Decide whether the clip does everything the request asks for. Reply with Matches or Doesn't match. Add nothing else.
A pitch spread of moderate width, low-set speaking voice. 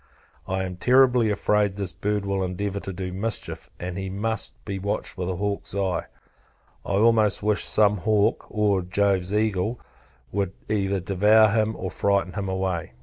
Doesn't match